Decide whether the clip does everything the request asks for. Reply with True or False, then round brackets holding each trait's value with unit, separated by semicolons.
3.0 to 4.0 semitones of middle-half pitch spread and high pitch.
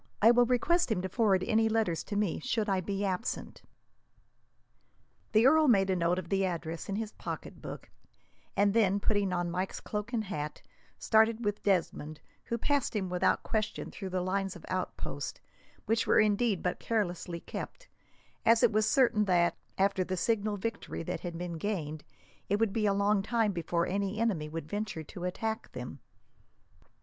True (3.5 semitones; 200 Hz)